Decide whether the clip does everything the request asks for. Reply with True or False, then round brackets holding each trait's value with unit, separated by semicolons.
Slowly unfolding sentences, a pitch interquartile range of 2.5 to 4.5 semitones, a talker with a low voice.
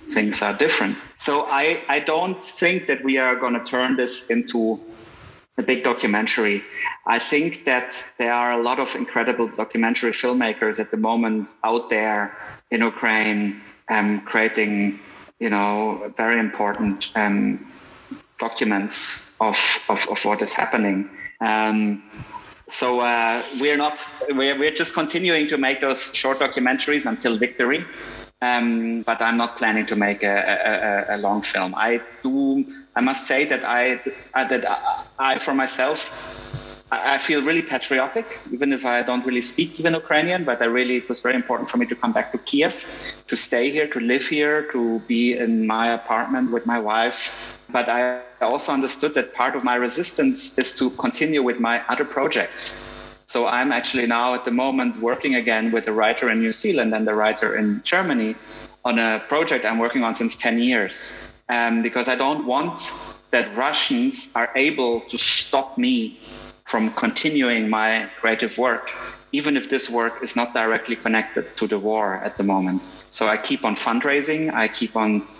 False (175 wpm; 3.6 semitones; 120 Hz)